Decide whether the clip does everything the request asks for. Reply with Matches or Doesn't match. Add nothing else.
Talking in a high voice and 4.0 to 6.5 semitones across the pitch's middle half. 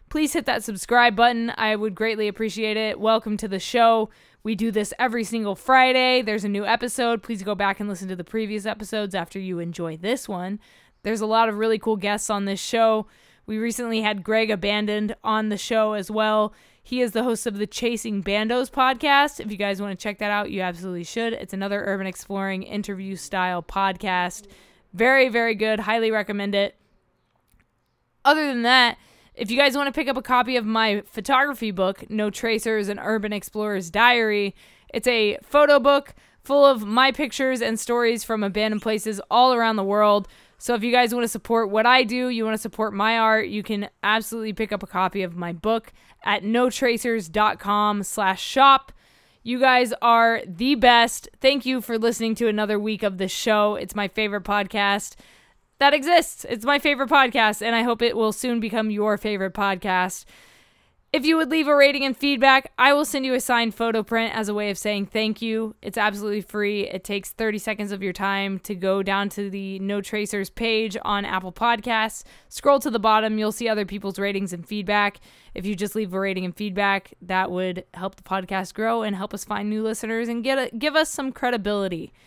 Doesn't match